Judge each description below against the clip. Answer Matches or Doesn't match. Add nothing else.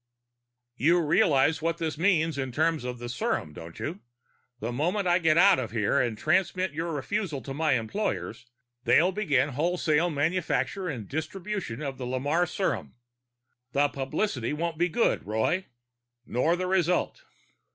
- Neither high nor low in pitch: Matches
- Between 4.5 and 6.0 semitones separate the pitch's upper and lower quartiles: Matches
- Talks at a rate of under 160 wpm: Matches